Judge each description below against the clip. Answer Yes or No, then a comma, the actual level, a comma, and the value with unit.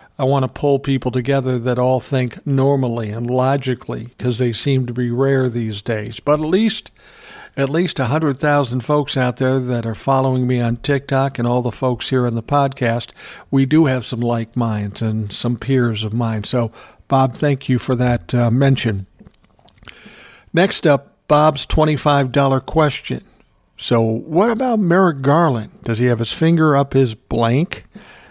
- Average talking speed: Yes, average, 175 wpm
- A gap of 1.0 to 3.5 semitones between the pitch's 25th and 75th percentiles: Yes, average, 2.8 semitones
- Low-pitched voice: Yes, low, 130 Hz